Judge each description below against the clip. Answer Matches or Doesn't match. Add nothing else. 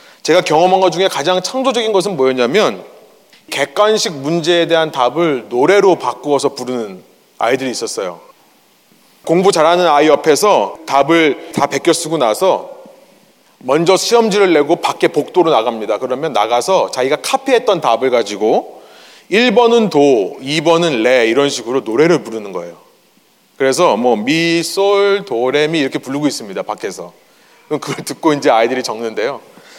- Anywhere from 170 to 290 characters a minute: Doesn't match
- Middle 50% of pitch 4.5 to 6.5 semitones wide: Matches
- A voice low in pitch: Doesn't match